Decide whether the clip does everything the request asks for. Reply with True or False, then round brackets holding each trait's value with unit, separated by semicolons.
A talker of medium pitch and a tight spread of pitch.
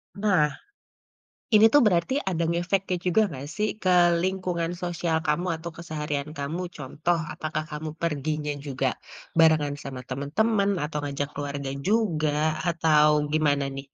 False (155 Hz; 3.1 semitones)